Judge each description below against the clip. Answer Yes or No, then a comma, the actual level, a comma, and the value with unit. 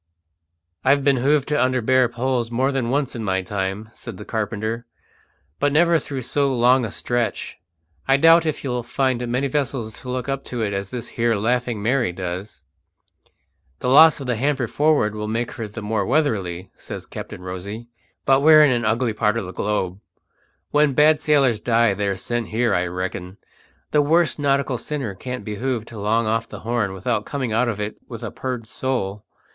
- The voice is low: Yes, low, 120 Hz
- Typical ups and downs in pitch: Yes, average, 4.2 semitones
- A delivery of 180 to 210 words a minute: Yes, average, 190 wpm